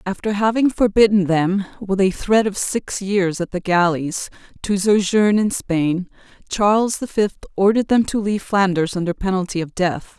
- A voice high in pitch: Yes, high, 195 Hz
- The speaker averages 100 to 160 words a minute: No, average, 170 wpm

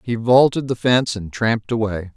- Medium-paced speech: Yes, average, 195 wpm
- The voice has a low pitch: Yes, low, 115 Hz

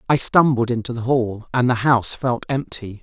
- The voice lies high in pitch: No, low, 120 Hz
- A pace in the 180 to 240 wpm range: Yes, average, 200 wpm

